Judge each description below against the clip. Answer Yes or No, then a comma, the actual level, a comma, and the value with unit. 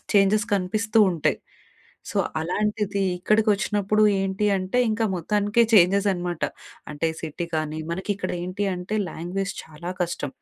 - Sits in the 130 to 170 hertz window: No, high, 195 Hz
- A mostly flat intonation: No, average, 3.1 semitones